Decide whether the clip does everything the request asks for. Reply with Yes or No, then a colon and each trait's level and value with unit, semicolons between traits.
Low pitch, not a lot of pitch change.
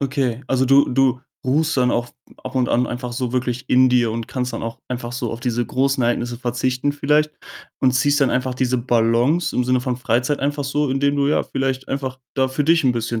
Yes: low, 130 Hz; narrow, 2.1 semitones